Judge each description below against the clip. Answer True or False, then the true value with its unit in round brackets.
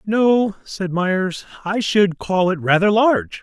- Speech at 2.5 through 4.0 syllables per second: True (3.6 syllables/s)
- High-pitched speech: True (195 Hz)